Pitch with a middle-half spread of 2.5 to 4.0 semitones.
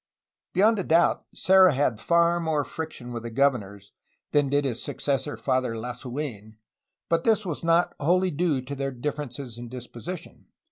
No: wide, 5.4 semitones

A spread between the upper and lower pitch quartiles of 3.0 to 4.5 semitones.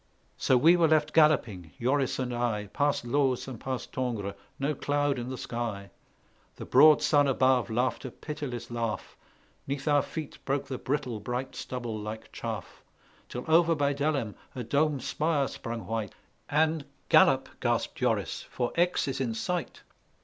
Yes: average, 3.6 semitones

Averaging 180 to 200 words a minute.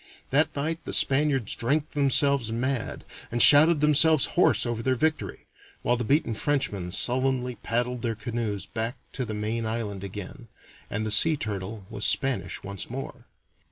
No: average, 155 wpm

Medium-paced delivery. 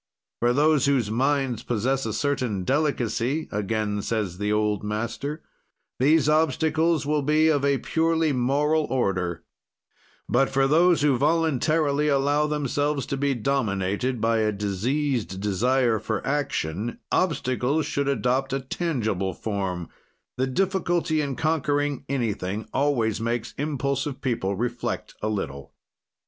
No: slow, 130 wpm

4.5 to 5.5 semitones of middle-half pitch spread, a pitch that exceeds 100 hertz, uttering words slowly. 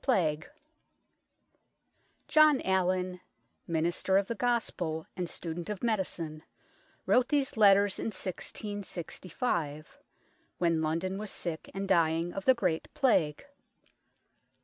No: average, 4.1 semitones; medium, 185 Hz; slow, 105 wpm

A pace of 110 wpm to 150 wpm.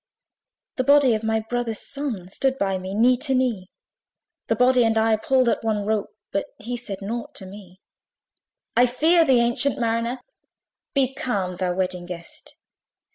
No: average, 165 wpm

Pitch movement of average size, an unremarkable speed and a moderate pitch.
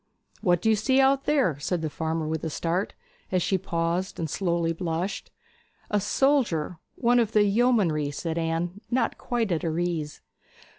Yes: average, 5.0 semitones; average, 175 wpm; medium, 175 Hz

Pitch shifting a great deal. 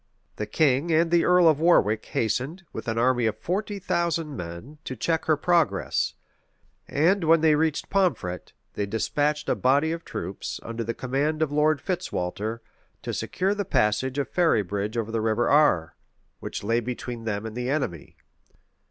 Yes: wide, 6.4 semitones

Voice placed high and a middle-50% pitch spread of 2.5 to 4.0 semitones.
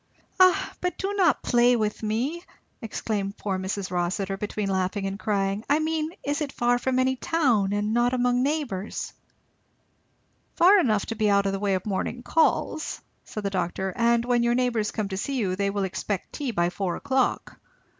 No: high, 220 Hz; average, 4.7 semitones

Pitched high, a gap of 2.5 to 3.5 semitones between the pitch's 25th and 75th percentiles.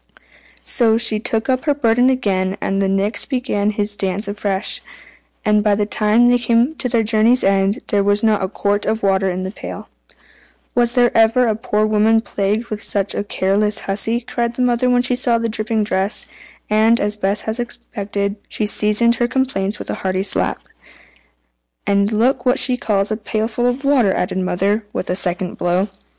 Yes: high, 215 Hz; average, 2.9 semitones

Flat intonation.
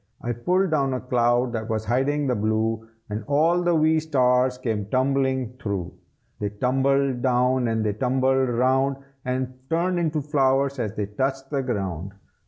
No: average, 3.4 semitones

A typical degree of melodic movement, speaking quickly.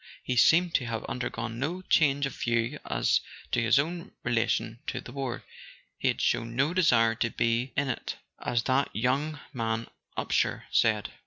No: average, 3.6 semitones; average, 170 wpm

